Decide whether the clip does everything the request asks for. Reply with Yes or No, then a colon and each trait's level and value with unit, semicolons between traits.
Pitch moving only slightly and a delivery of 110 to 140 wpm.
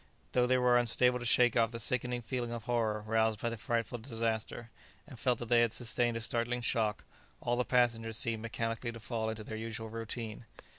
No: narrow, 1.5 semitones; fast, 205 wpm